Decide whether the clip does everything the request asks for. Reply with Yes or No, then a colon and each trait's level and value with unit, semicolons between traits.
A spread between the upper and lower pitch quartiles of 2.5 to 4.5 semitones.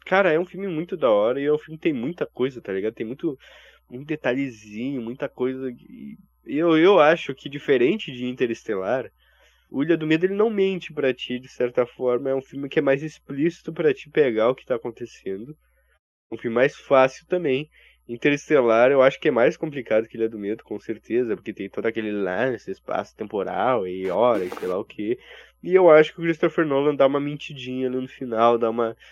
No: average, 5.3 semitones